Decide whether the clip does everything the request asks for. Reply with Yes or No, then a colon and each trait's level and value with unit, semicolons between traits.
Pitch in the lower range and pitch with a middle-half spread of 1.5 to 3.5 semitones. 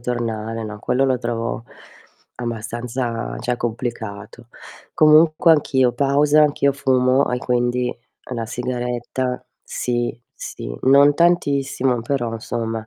Yes: low, 125 Hz; narrow, 2.6 semitones